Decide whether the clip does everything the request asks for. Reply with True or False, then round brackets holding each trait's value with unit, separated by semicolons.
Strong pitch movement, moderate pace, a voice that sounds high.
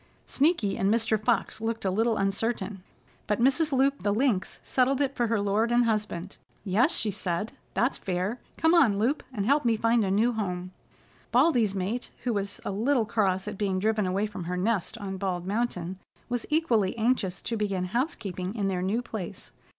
False (3.8 semitones; 190 wpm; 215 Hz)